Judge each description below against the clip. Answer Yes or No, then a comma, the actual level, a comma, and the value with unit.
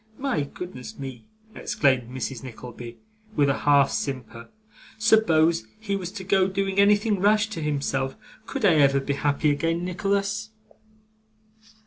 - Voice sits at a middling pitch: Yes, medium, 160 Hz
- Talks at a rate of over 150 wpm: No, slow, 135 wpm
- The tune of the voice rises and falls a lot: Yes, wide, 6.6 semitones